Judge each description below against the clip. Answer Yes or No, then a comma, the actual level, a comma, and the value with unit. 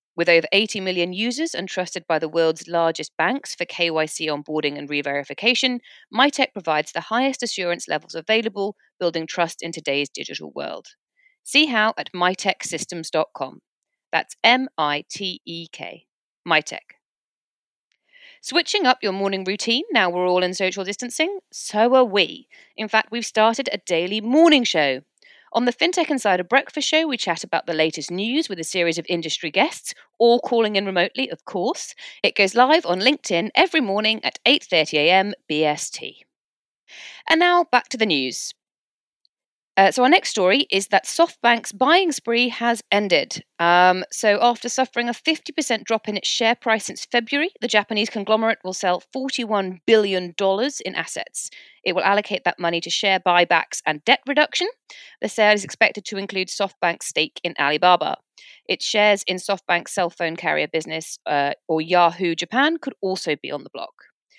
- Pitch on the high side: Yes, high, 200 Hz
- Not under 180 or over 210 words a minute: No, average, 165 wpm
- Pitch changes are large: Yes, wide, 6.1 semitones